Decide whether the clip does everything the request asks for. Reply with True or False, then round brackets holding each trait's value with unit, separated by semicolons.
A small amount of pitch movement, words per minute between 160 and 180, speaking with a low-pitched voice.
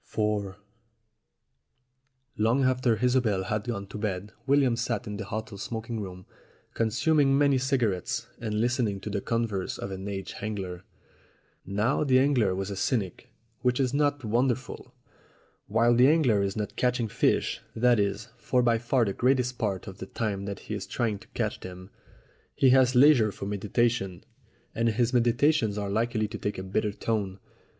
False (3.8 semitones; 165 wpm; 110 Hz)